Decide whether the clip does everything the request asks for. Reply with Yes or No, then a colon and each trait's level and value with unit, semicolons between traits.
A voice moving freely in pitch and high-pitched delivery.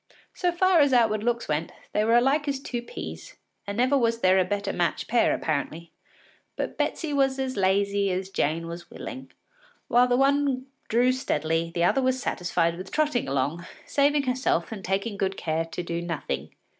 Yes: wide, 7.2 semitones; high, 210 Hz